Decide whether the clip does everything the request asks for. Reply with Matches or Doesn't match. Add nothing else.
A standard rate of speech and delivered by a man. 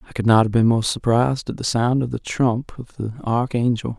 Doesn't match